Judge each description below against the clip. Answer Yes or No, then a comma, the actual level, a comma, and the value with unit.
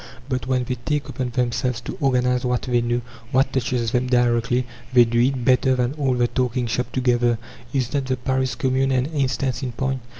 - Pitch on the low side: Yes, low, 125 Hz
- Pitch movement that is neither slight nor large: No, narrow, 1.3 semitones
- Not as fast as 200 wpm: No, fast, 205 wpm